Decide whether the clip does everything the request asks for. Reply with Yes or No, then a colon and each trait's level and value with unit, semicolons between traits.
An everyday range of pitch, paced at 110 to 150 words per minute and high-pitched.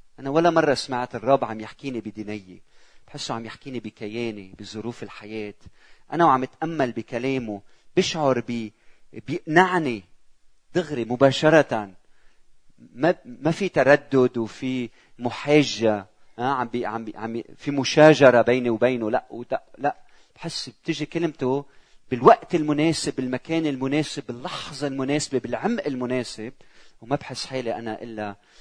No: average, 4.6 semitones; average, 120 wpm; low, 130 Hz